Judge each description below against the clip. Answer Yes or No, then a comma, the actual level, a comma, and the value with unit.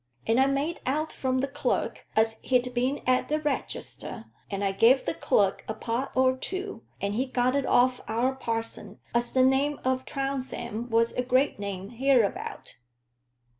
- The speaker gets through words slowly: No, average, 170 wpm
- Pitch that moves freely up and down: No, average, 2.8 semitones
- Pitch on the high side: Yes, very high, 255 Hz